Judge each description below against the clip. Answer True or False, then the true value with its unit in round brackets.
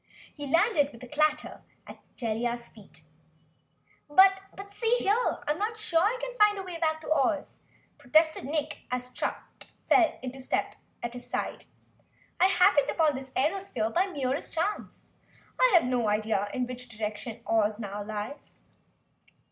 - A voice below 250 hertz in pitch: False (290 Hz)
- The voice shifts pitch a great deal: True (7.2 semitones)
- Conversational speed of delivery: True (165 wpm)